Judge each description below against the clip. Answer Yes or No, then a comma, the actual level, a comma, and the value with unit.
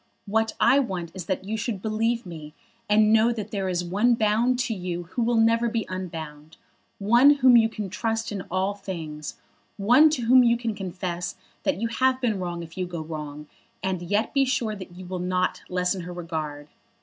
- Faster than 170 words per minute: Yes, average, 200 wpm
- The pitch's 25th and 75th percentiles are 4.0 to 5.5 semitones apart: Yes, average, 4.5 semitones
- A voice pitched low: No, high, 200 Hz